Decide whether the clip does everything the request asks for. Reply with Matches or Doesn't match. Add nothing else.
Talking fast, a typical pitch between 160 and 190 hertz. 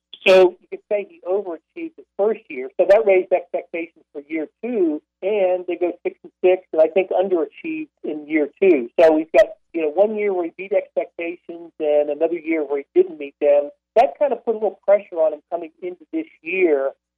Matches